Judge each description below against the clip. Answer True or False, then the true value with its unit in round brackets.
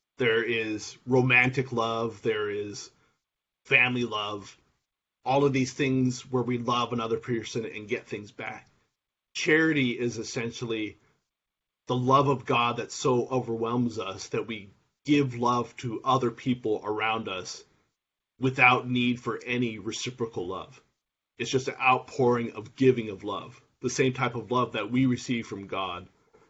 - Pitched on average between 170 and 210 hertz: False (120 Hz)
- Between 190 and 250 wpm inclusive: False (145 wpm)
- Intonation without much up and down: True (2.0 semitones)